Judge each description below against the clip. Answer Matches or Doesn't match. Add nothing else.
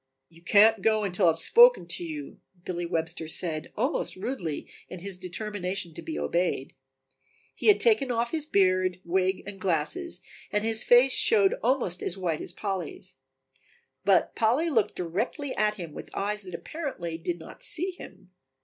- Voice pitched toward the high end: Matches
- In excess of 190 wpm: Doesn't match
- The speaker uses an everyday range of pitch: Doesn't match